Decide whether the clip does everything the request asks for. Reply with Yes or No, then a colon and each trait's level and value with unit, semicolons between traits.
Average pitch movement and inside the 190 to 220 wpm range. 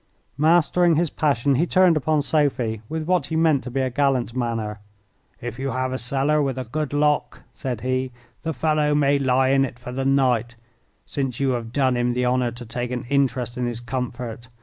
Yes: average, 3.2 semitones; fast, 205 wpm